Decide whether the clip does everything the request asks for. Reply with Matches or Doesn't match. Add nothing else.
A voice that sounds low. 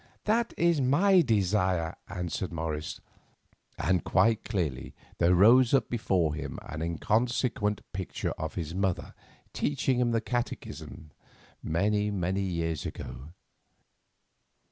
Matches